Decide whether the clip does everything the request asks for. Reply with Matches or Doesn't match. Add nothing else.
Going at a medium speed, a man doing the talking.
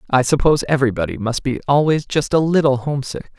Matches